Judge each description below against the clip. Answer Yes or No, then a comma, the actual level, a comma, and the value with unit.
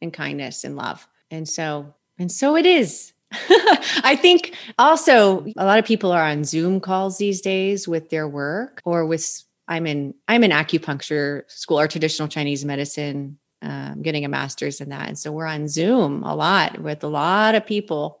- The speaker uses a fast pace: No, average, 185 wpm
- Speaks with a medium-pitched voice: Yes, medium, 165 Hz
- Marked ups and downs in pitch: Yes, wide, 5.9 semitones